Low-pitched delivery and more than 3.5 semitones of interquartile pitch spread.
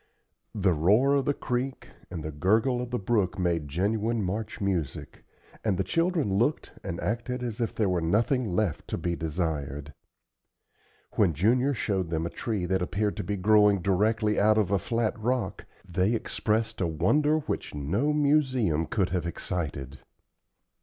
Yes: low, 100 Hz; average, 5.3 semitones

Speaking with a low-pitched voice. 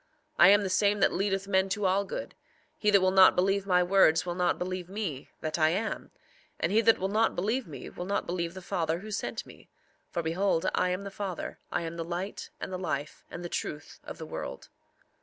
No: medium, 185 Hz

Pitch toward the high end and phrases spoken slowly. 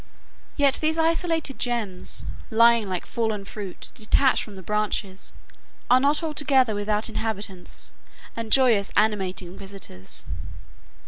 Yes: high, 220 Hz; slow, 115 wpm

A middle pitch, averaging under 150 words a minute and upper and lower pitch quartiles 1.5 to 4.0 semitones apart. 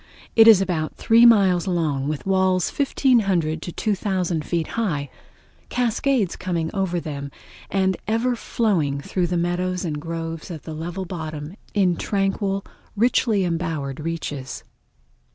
Yes: medium, 180 Hz; slow, 135 wpm; average, 3.6 semitones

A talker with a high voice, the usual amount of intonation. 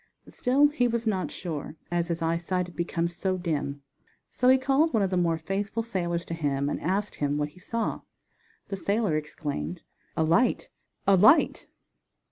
No: medium, 180 Hz; average, 5.0 semitones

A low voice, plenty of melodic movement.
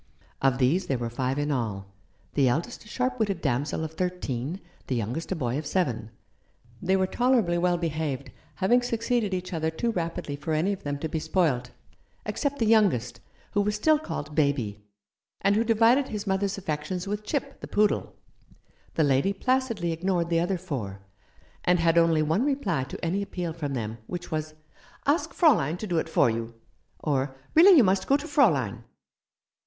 No: medium, 170 Hz; wide, 6.5 semitones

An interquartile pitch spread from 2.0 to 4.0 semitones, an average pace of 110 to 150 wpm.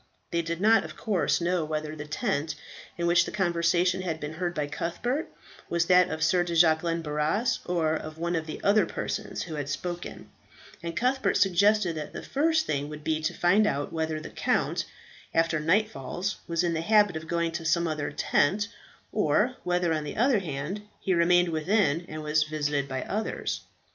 No: average, 2.9 semitones; average, 190 wpm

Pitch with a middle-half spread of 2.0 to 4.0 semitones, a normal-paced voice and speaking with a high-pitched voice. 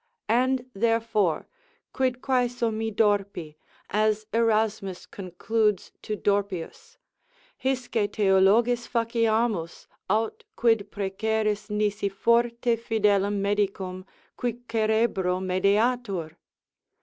No: average, 2.7 semitones; slow, 85 wpm; high, 215 Hz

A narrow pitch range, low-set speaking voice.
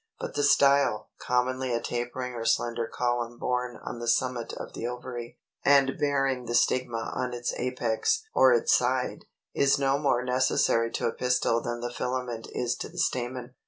Yes: narrow, 1.5 semitones; low, 125 Hz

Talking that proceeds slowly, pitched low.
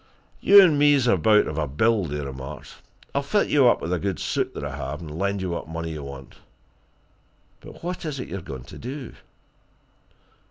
No: average, 200 wpm; very low, 95 Hz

